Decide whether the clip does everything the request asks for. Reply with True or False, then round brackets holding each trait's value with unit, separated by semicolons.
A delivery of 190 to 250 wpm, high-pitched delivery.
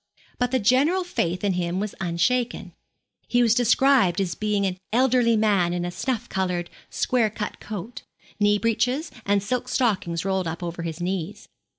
False (165 wpm; 205 Hz)